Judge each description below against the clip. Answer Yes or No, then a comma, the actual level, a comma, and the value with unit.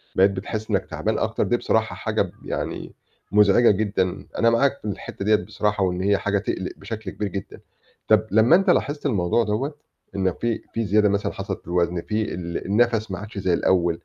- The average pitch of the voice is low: Yes, low, 105 Hz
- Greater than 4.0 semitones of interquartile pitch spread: No, average, 2.7 semitones